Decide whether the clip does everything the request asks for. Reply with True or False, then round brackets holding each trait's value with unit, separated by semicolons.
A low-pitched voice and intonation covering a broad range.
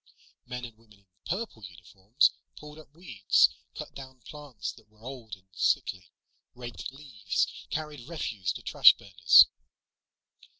True (120 Hz; 6.3 semitones)